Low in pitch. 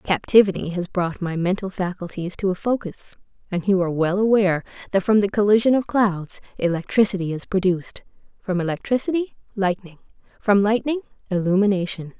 No: high, 195 Hz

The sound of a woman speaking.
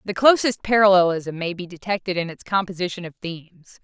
Yes: female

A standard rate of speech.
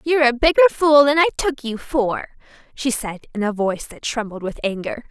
No: fast, 210 wpm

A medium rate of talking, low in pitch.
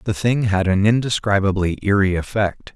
Yes: average, 155 wpm; low, 100 Hz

